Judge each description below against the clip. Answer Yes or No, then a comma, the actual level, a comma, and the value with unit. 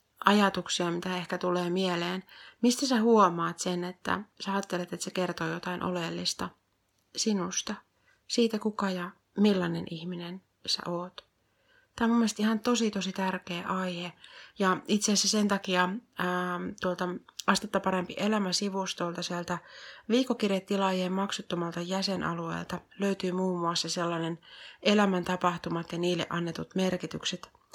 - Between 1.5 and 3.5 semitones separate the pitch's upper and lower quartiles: Yes, narrow, 2.5 semitones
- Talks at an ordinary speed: Yes, average, 125 wpm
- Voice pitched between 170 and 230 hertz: Yes, medium, 185 Hz